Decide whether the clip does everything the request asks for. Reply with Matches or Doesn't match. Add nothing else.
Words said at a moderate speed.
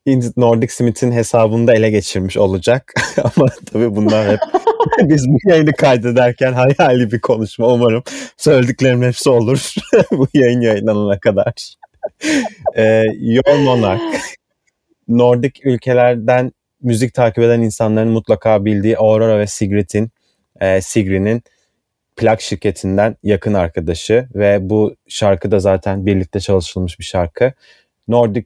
Matches